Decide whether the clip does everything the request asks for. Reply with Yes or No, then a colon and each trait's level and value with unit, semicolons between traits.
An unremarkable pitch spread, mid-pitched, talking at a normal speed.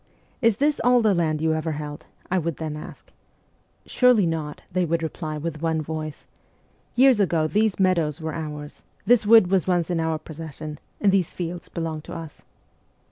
Yes: average, 3.4 semitones; medium, 165 Hz; average, 190 wpm